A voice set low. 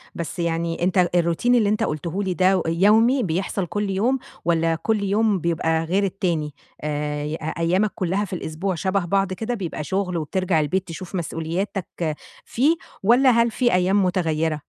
No: medium, 185 Hz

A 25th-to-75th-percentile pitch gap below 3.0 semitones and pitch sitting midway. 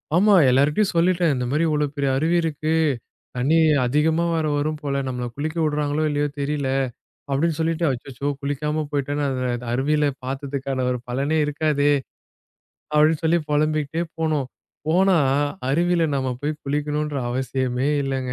Yes: narrow, 2.4 semitones; medium, 150 Hz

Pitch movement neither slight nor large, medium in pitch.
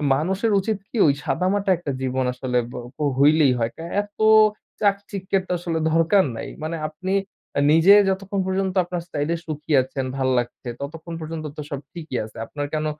Yes: average, 5.0 semitones; medium, 165 Hz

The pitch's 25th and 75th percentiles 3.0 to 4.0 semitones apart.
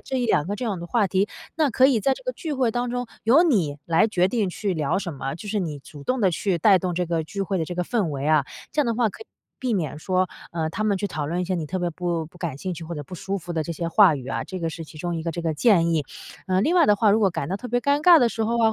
No: wide, 5.5 semitones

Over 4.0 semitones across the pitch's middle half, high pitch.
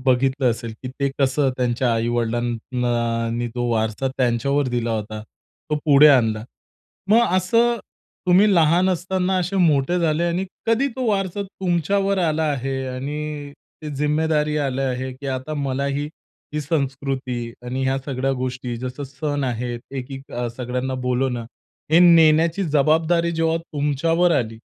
No: average, 4.5 semitones; medium, 140 Hz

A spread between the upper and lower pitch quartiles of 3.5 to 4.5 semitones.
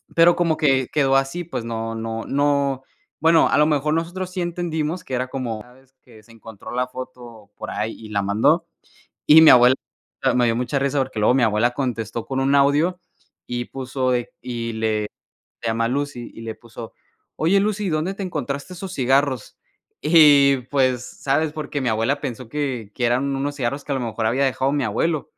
Yes: average, 4.0 semitones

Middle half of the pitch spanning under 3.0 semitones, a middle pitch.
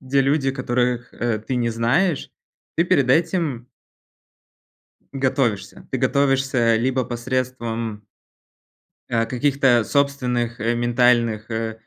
No: narrow, 2.5 semitones; low, 125 Hz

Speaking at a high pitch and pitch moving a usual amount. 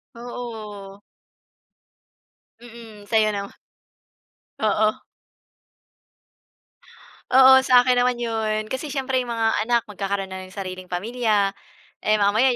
Yes: high, 220 Hz; average, 3.3 semitones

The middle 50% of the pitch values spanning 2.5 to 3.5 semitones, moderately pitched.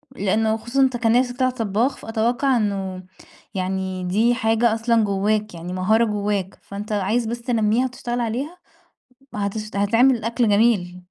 No: average, 3.0 semitones; high, 220 Hz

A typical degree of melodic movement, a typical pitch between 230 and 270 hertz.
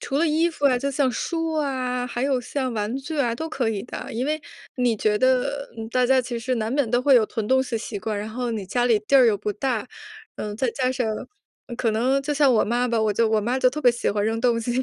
Yes: average, 3.0 semitones; very high, 250 Hz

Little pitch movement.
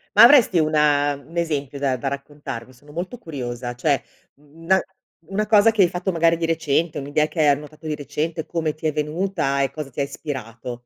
No: average, 3.1 semitones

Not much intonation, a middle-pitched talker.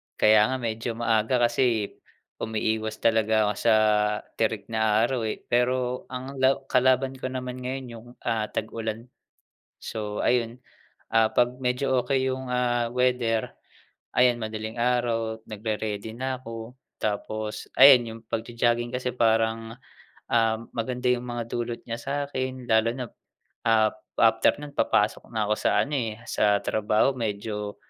No: narrow, 2.2 semitones; low, 115 Hz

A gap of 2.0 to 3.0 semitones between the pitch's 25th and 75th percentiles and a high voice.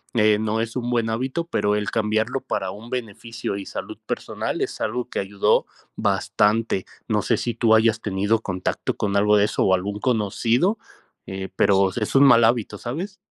No: narrow, 2.6 semitones; low, 110 Hz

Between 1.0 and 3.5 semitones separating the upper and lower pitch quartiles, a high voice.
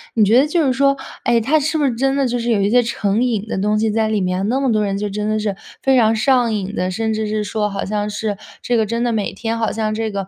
Yes: average, 2.7 semitones; high, 220 Hz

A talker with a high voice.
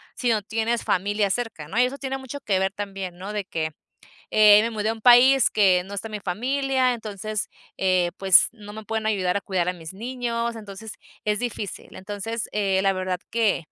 Yes: high, 210 Hz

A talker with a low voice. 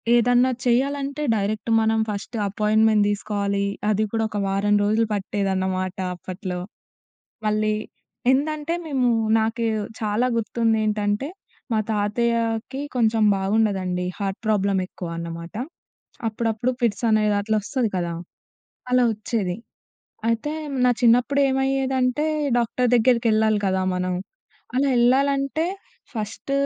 No: high, 220 Hz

